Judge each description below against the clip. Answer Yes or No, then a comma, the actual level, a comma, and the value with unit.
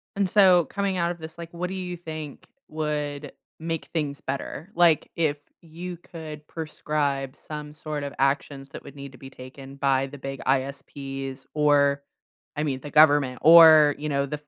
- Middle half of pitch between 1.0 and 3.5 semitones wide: Yes, average, 2.8 semitones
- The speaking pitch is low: No, medium, 150 Hz